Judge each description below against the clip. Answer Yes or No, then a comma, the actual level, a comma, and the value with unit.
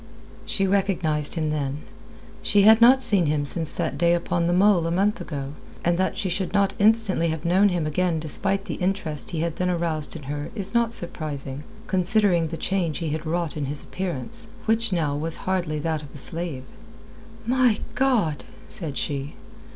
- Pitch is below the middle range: No, medium, 170 Hz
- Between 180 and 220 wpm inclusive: Yes, average, 185 wpm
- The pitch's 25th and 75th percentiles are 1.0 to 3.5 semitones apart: No, average, 4.3 semitones